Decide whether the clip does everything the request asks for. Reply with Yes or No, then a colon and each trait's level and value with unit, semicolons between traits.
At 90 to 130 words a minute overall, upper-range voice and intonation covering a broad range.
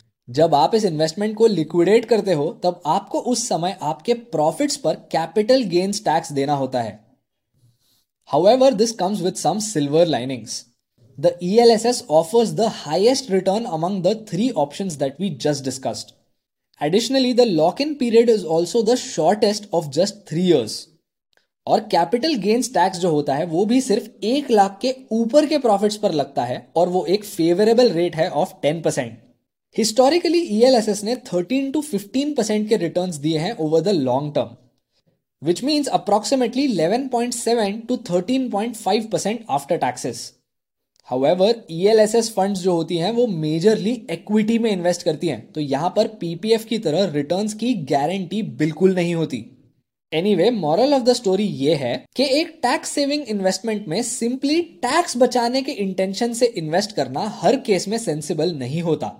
No: average, 160 wpm; high, 195 Hz; wide, 6.5 semitones